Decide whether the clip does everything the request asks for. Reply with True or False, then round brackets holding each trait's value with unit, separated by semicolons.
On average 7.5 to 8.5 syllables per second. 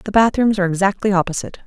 True (7.6 syllables/s)